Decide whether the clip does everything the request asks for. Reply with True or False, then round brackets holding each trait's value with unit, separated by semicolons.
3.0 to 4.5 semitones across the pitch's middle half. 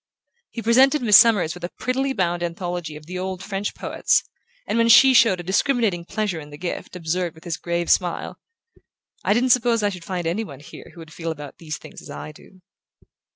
False (5.1 semitones)